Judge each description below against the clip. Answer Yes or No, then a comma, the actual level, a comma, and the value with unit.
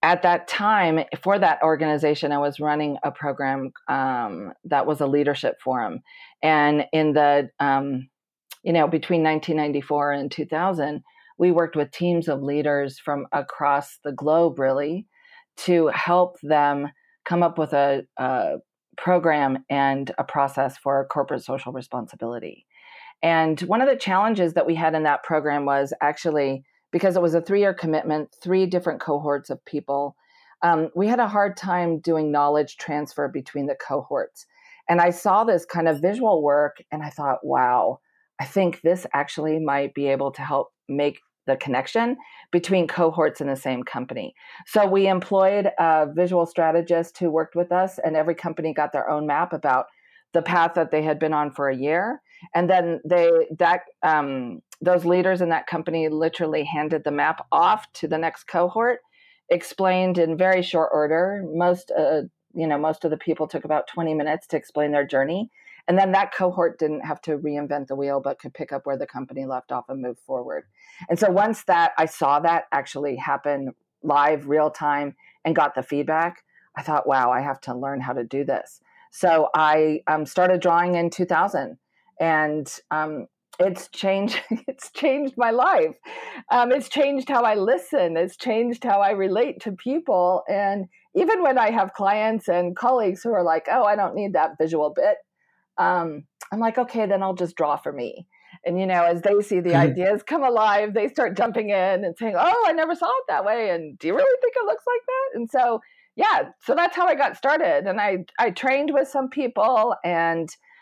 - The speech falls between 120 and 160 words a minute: No, average, 185 wpm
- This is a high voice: No, medium, 165 Hz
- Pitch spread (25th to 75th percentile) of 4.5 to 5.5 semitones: Yes, average, 5.2 semitones